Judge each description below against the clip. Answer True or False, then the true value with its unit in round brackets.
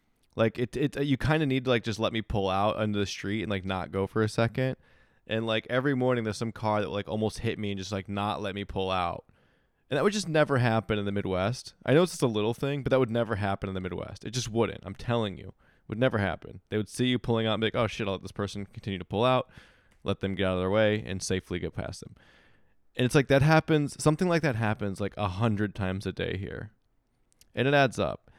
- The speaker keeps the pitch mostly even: False (4.1 semitones)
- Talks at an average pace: False (275 wpm)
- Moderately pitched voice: False (110 Hz)